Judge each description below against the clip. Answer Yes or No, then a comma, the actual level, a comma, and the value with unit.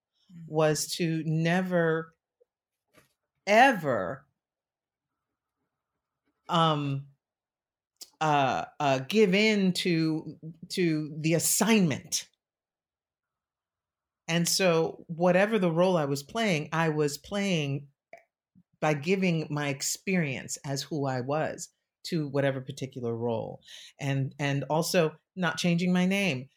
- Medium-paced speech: No, slow, 95 wpm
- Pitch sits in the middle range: Yes, medium, 160 Hz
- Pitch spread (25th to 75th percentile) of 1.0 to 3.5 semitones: No, average, 3.9 semitones